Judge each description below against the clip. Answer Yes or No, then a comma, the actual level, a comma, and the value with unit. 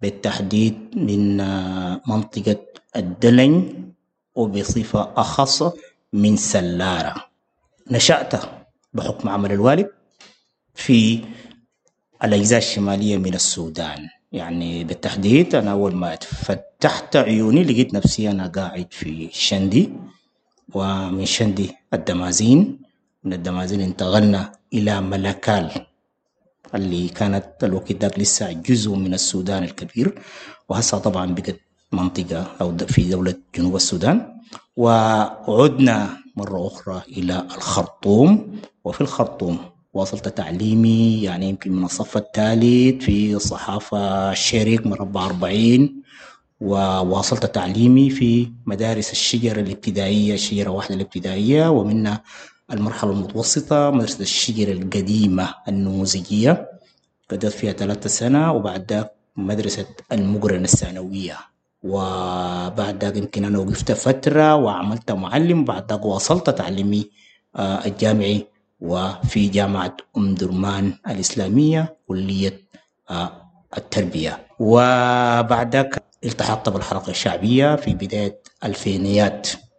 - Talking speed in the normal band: No, slow, 95 wpm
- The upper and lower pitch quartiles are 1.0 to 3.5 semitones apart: Yes, average, 3.2 semitones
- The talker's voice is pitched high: No, low, 100 Hz